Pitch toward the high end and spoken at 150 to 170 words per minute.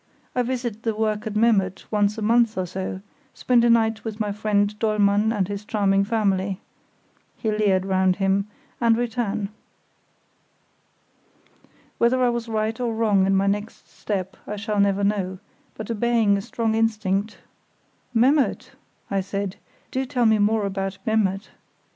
Yes: high, 210 Hz; average, 155 wpm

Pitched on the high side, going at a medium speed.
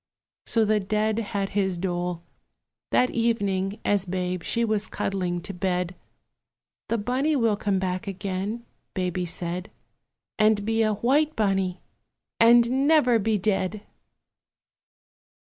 No: high, 205 Hz; slow, 125 wpm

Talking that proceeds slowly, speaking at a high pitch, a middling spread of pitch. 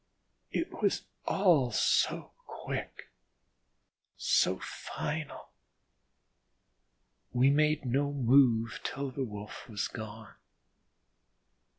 No: slow, 80 wpm; low, 130 Hz; average, 4.1 semitones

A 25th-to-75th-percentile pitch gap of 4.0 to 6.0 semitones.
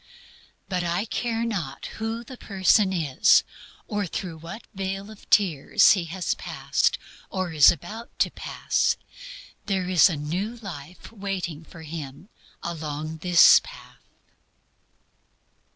Yes: average, 4.3 semitones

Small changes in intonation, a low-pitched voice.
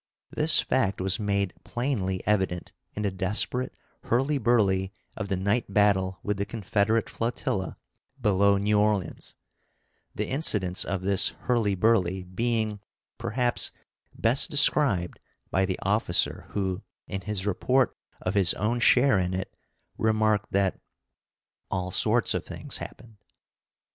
No: average, 3.4 semitones; low, 100 Hz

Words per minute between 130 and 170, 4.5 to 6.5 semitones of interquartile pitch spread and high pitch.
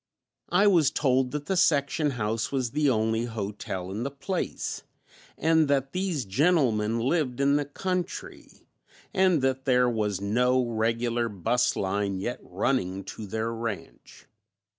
No: average, 140 wpm; average, 4.8 semitones; low, 125 Hz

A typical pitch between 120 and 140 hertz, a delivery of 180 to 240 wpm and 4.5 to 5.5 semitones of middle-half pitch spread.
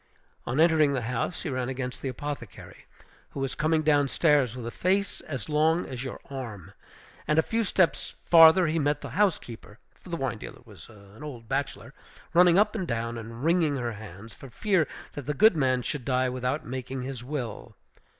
Yes: low, 135 Hz; average, 195 wpm; average, 4.8 semitones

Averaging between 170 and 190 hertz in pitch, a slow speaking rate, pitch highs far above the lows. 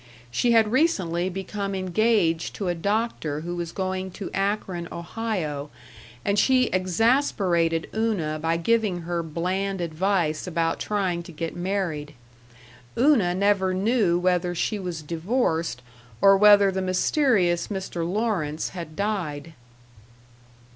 No: medium, 185 Hz; slow, 125 wpm; average, 3.5 semitones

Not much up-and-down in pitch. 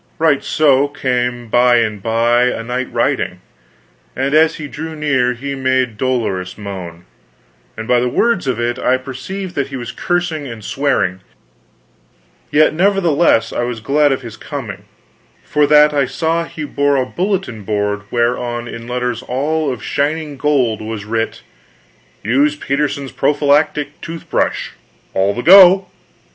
No: average, 4.0 semitones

